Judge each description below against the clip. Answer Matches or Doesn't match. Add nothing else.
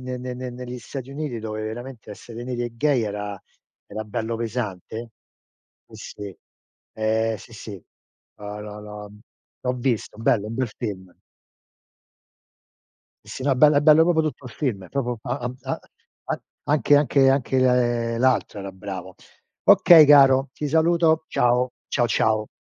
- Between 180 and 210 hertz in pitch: Doesn't match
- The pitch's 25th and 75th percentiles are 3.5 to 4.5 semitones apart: Matches